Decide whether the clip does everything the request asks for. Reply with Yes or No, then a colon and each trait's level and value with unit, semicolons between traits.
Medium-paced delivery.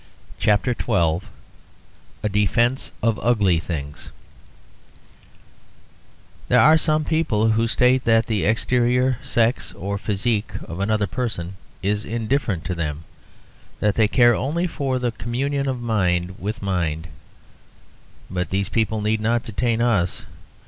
No: slow, 120 wpm